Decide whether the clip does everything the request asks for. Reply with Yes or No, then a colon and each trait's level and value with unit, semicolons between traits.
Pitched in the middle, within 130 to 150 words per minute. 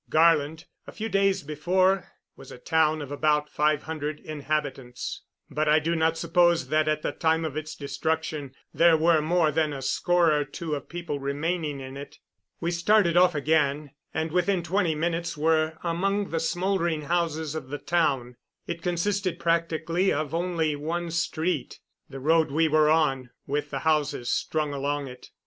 No: medium, 160 Hz; average, 170 wpm